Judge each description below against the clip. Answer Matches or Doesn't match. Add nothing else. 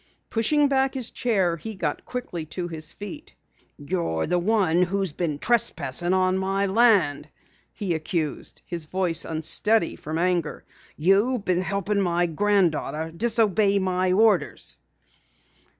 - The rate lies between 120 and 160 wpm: Matches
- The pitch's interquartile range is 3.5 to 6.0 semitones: Matches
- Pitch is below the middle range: Doesn't match